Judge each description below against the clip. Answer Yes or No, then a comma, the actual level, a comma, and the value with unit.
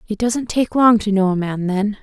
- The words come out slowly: No, fast, 265 wpm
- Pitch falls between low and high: No, high, 210 Hz